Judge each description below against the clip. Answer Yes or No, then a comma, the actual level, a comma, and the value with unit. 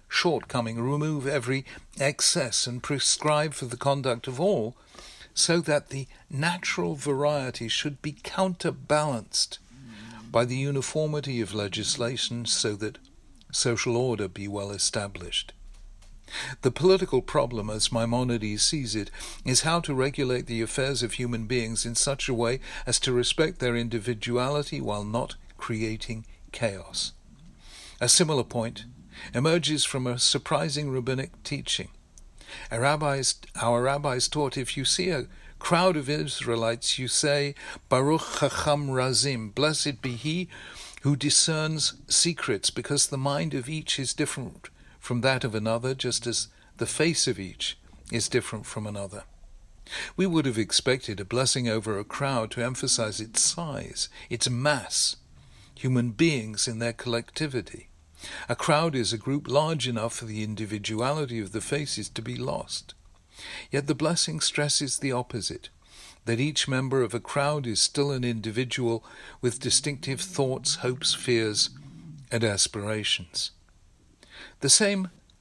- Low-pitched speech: Yes, low, 125 Hz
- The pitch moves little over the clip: No, average, 4.1 semitones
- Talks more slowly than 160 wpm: Yes, average, 140 wpm